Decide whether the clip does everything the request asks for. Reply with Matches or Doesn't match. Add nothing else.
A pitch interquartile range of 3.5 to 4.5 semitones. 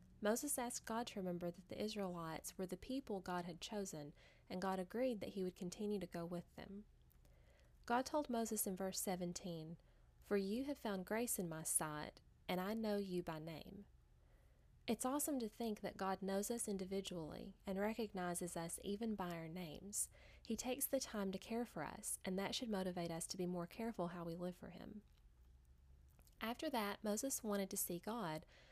Matches